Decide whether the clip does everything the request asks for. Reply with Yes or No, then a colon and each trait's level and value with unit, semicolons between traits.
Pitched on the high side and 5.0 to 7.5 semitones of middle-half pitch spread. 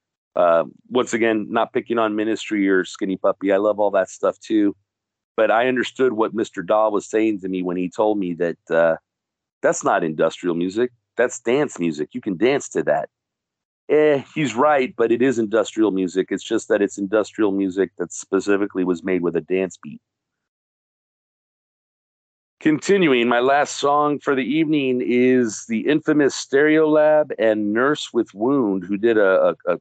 No: low, 110 Hz; wide, 5.5 semitones